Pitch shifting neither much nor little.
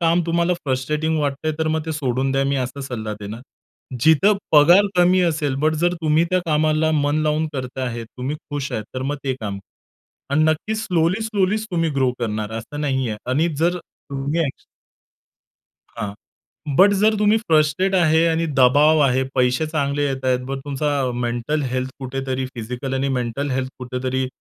Yes: average, 3.7 semitones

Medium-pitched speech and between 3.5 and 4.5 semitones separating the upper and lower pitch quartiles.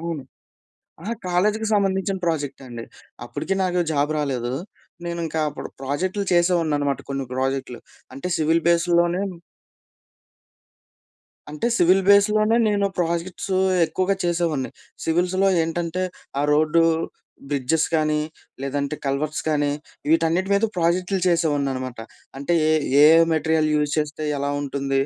Yes: medium, 160 Hz; average, 3.9 semitones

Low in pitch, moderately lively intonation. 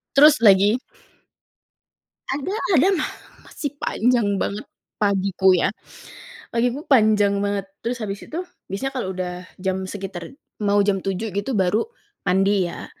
No: high, 200 Hz; average, 3.9 semitones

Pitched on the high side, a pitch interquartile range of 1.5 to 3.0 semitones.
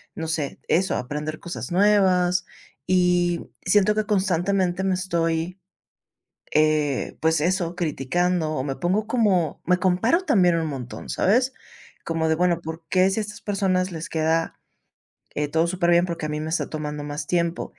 No: medium, 175 Hz; average, 2.7 semitones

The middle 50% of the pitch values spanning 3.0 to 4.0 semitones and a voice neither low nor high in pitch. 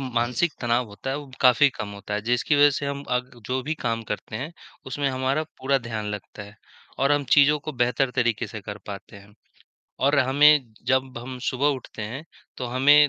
No: average, 3.3 semitones; low, 130 Hz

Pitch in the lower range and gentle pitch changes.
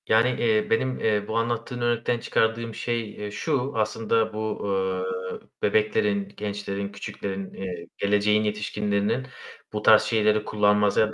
Yes: low, 110 Hz; narrow, 1.8 semitones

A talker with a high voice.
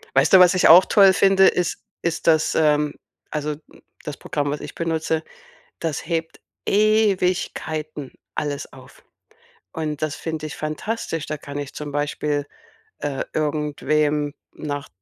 No: medium, 155 Hz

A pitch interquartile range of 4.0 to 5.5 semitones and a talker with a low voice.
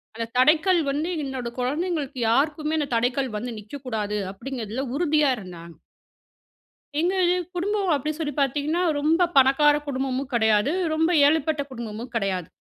No: average, 4.6 semitones; very high, 275 Hz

